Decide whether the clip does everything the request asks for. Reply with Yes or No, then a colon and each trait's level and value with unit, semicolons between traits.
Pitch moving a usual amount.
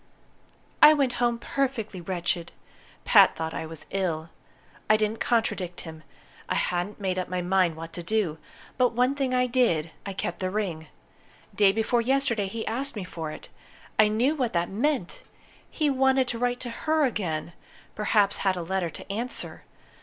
No: wide, 5.8 semitones